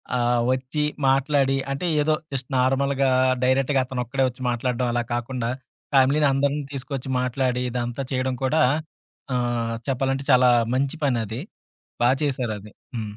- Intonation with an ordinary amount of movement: No, narrow, 2.0 semitones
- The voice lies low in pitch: Yes, low, 130 Hz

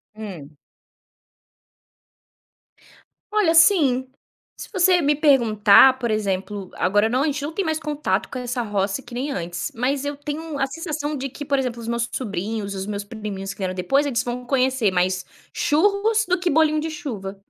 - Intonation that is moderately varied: No, wide, 6.4 semitones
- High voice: Yes, very high, 255 Hz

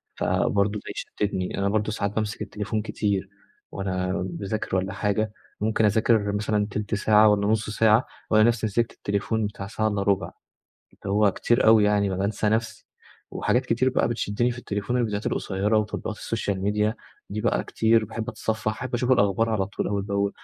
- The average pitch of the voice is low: Yes, low, 105 Hz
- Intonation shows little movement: Yes, narrow, 1.7 semitones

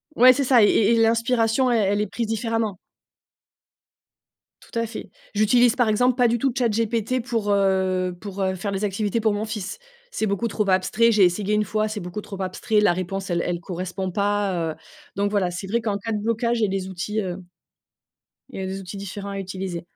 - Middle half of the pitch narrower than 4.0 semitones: Yes, average, 3.0 semitones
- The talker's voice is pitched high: Yes, high, 205 Hz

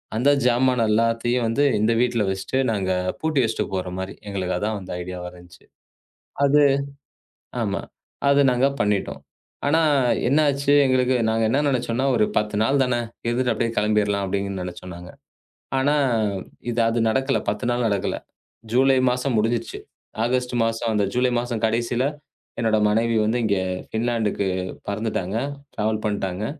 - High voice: No, low, 115 Hz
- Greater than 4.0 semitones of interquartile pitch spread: No, average, 3.5 semitones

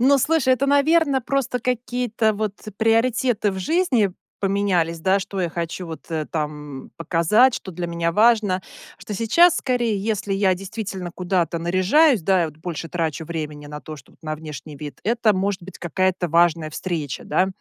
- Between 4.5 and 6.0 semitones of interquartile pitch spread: Yes, wide, 5.5 semitones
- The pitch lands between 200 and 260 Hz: No, high, 190 Hz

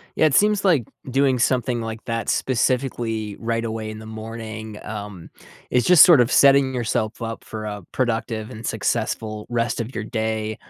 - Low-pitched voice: Yes, low, 115 Hz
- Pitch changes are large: No, narrow, 2.6 semitones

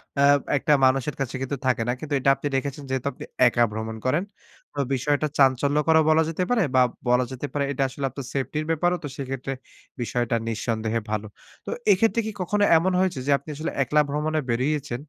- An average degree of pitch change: Yes, average, 3.2 semitones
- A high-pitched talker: No, medium, 140 Hz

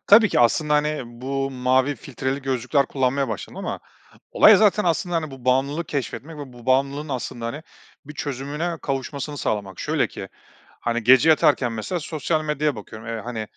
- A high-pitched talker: No, low, 135 Hz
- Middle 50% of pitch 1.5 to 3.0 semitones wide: No, average, 3.5 semitones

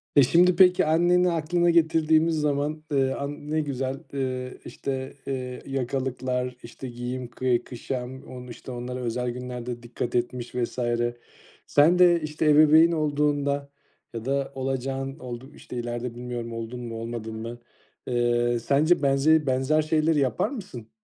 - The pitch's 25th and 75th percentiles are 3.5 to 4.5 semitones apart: Yes, average, 3.8 semitones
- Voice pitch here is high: No, low, 135 Hz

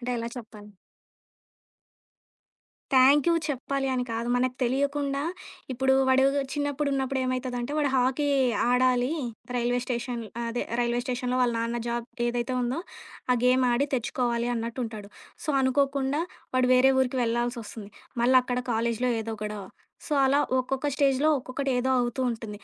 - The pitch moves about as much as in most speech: No, narrow, 2.1 semitones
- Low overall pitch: No, very high, 250 Hz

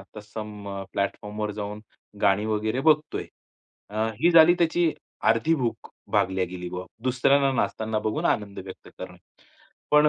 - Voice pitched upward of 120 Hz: No, low, 110 Hz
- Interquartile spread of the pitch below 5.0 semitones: No, average, 5.3 semitones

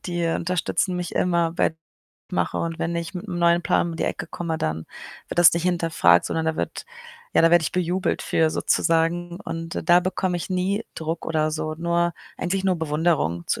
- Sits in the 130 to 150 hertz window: No, medium, 170 Hz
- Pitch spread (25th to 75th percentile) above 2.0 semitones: No, narrow, 1.4 semitones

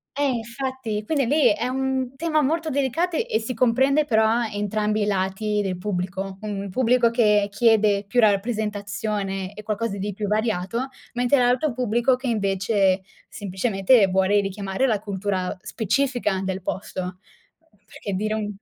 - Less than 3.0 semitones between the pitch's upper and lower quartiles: No, average, 3.8 semitones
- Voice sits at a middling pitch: No, high, 215 Hz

